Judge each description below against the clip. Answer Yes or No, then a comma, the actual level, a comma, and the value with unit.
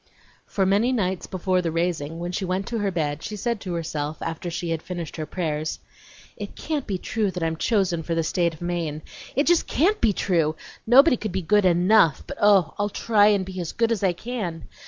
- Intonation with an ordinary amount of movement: Yes, average, 4.1 semitones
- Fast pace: Yes, fast, 220 wpm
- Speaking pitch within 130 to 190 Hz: Yes, medium, 185 Hz